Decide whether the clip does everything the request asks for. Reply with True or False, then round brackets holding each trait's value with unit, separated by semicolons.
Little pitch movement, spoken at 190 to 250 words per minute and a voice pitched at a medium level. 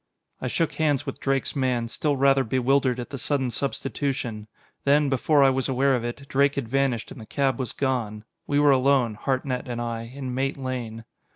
False (2.3 semitones; 195 wpm; 130 Hz)